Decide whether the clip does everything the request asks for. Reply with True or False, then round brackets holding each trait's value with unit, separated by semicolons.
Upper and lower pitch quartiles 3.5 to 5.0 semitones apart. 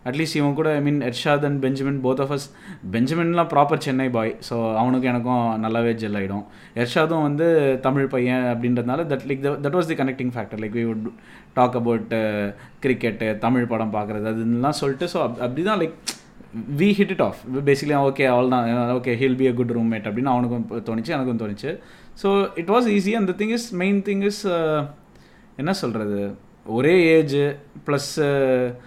True (4.3 semitones)